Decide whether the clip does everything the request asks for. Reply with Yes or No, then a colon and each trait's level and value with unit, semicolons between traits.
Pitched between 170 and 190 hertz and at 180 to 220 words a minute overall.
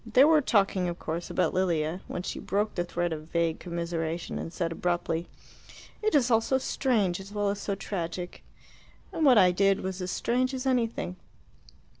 Yes: medium, 185 Hz; average, 185 wpm